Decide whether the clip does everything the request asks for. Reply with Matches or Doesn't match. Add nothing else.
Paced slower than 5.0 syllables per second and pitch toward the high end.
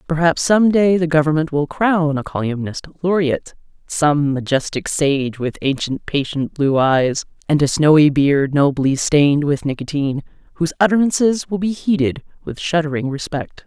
Doesn't match